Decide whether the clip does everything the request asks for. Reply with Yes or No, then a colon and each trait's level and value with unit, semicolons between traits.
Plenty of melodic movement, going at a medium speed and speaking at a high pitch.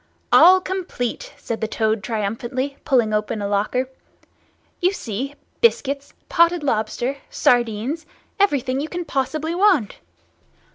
No: wide, 7.0 semitones; slow, 105 wpm; very high, 265 Hz